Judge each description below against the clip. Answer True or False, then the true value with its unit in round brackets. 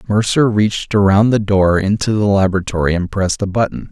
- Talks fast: False (185 wpm)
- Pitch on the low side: True (100 Hz)